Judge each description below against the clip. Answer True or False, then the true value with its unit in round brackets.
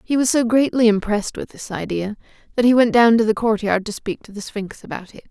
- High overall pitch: True (220 Hz)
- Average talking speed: False (260 wpm)